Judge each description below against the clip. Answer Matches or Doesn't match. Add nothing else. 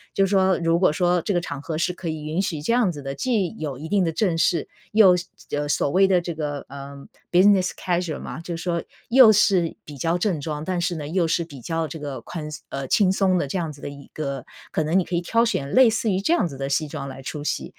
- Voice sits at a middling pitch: Matches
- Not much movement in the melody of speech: Doesn't match